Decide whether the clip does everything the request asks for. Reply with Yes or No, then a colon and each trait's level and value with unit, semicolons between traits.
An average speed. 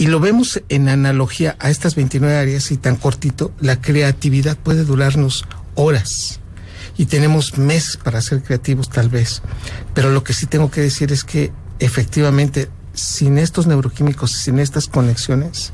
Yes: average, 155 wpm